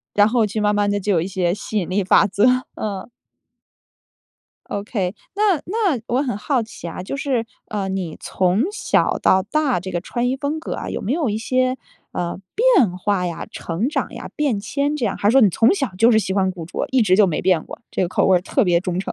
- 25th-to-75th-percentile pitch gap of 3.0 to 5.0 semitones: No, wide, 5.5 semitones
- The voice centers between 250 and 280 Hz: No, high, 205 Hz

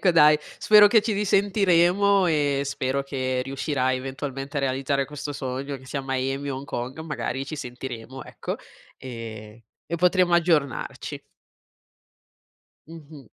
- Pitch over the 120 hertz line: Yes, medium, 140 Hz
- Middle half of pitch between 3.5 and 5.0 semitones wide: Yes, average, 4.1 semitones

